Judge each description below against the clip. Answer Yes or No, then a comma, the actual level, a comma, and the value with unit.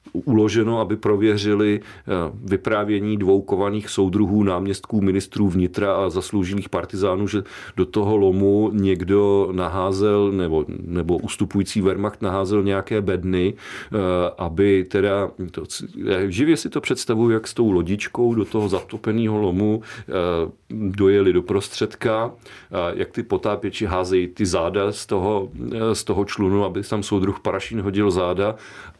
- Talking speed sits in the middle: Yes, average, 125 wpm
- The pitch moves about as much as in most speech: No, narrow, 1.7 semitones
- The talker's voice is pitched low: Yes, low, 100 Hz